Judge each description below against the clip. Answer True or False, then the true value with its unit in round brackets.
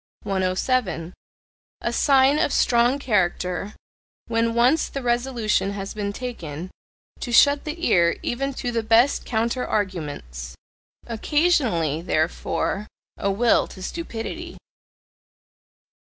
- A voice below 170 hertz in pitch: False (230 Hz)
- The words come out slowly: True (110 wpm)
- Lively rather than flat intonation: True (5.7 semitones)